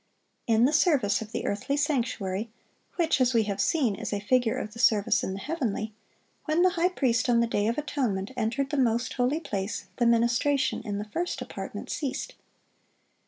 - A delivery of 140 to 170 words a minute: No, average, 190 wpm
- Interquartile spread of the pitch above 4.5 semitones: Yes, average, 4.9 semitones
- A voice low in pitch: No, high, 235 Hz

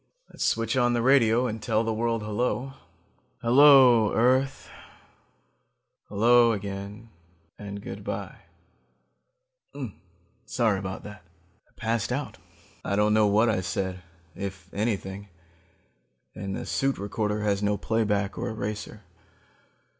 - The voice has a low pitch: Yes, low, 110 Hz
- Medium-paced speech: No, slow, 120 wpm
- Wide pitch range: No, average, 2.7 semitones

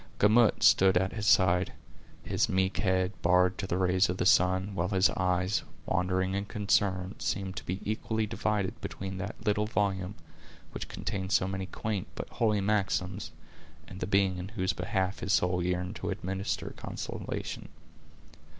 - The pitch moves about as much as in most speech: No, narrow, 1.7 semitones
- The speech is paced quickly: No, average, 160 wpm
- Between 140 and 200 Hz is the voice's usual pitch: No, very low, 95 Hz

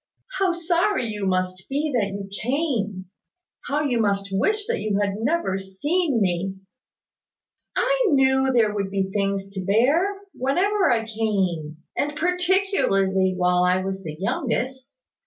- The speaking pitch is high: Yes, high, 220 Hz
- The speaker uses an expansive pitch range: Yes, wide, 7.8 semitones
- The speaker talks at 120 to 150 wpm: Yes, average, 145 wpm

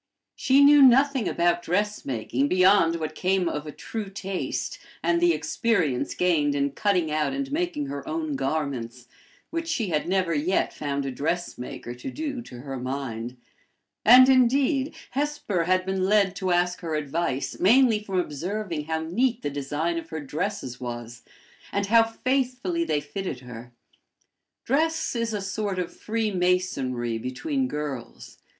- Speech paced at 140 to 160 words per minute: Yes, average, 150 wpm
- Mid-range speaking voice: Yes, medium, 180 Hz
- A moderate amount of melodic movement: No, wide, 8.0 semitones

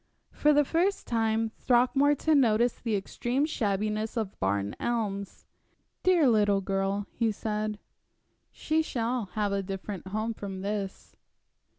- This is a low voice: No, high, 220 Hz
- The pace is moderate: No, slow, 125 wpm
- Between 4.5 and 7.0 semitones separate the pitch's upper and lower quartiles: No, average, 3.7 semitones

